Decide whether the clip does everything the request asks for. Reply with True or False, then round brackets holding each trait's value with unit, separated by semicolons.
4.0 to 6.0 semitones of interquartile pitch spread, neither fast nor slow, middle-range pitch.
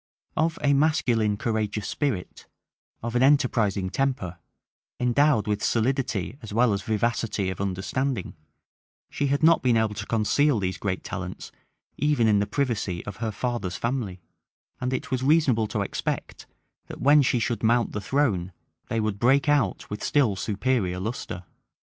False (4.7 semitones; 155 wpm; 115 Hz)